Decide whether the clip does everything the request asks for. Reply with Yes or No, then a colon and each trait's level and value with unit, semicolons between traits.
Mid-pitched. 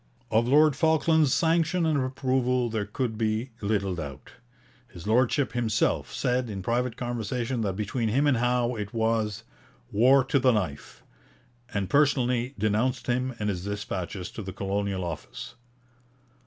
No: low, 115 Hz